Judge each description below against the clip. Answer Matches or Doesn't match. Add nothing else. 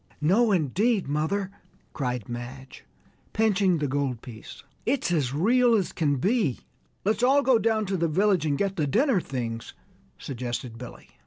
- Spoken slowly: Doesn't match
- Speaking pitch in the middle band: Matches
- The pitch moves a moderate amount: Doesn't match